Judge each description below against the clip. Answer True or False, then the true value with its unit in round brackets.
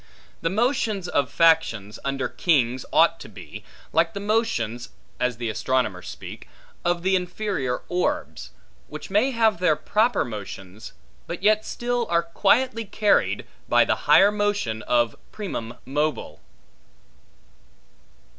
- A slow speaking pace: True (125 wpm)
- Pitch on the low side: False (170 Hz)